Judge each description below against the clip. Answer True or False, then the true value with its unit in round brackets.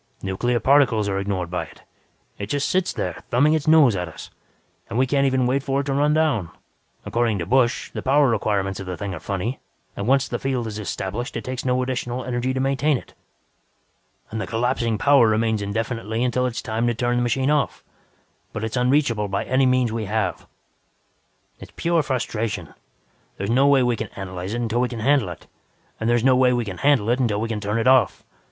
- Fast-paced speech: True (215 wpm)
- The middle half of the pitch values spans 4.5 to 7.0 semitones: False (3.7 semitones)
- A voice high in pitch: False (120 Hz)